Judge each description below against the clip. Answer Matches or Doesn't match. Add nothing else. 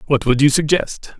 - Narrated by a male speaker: Matches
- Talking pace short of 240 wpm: Matches